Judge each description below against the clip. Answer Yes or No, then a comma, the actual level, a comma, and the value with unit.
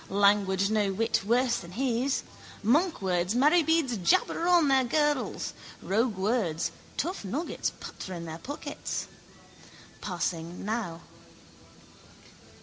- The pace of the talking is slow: Yes, slow, 100 wpm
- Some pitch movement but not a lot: No, wide, 6.3 semitones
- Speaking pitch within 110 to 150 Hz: No, high, 220 Hz